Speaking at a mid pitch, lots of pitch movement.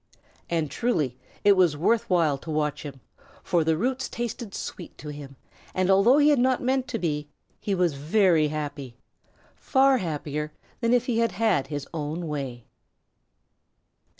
Yes: medium, 170 Hz; wide, 7.5 semitones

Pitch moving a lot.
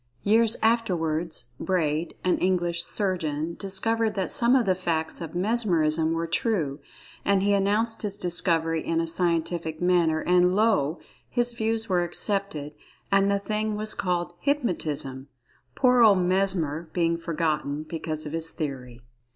No: average, 4.1 semitones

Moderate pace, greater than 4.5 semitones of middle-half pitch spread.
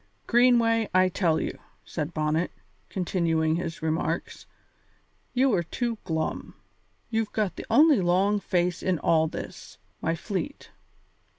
No: slow, 125 wpm; wide, 5.4 semitones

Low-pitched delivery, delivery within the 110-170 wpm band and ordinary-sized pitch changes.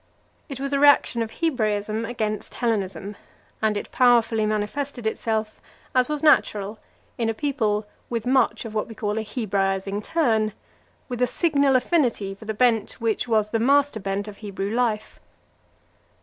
No: high, 225 Hz; average, 160 wpm; average, 3.1 semitones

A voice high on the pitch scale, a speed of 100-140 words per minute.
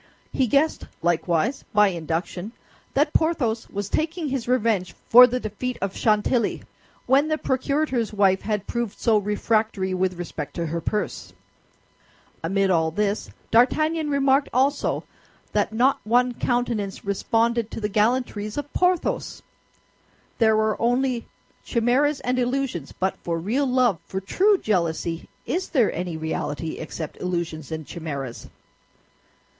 Yes: high, 220 Hz; slow, 135 wpm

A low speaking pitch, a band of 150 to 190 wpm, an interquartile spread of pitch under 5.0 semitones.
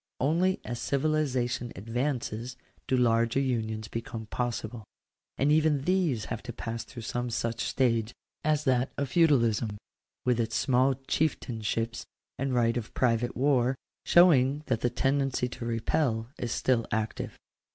No: low, 125 Hz; average, 140 wpm; average, 3.0 semitones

